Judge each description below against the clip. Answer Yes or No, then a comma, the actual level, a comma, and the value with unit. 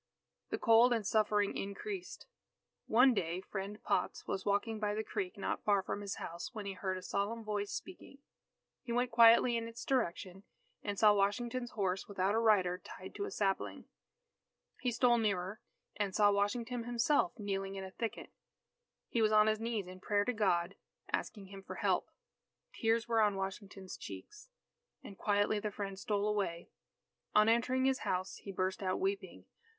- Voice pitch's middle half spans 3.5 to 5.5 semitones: No, average, 3.0 semitones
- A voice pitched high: Yes, high, 210 Hz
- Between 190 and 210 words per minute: No, average, 175 wpm